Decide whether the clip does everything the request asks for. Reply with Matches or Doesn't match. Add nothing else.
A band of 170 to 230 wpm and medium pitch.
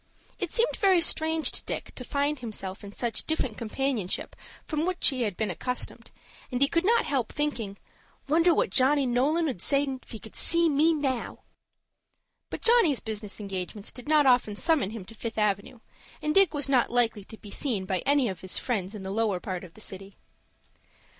Doesn't match